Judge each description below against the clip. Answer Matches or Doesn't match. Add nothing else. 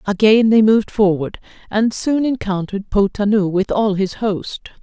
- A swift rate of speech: Doesn't match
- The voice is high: Matches